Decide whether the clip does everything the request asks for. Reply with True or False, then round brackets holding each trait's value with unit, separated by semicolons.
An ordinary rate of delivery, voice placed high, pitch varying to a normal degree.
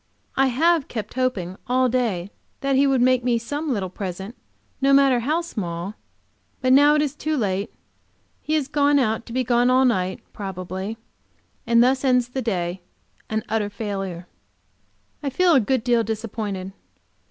True (165 wpm; 240 Hz; 4.9 semitones)